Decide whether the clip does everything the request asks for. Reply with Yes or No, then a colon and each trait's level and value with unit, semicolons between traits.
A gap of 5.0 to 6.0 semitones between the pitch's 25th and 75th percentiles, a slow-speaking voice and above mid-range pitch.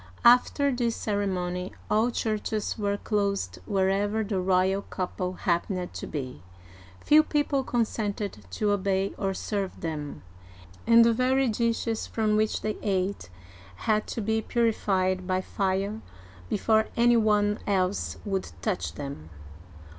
No: average, 2.9 semitones; slow, 130 wpm; high, 205 Hz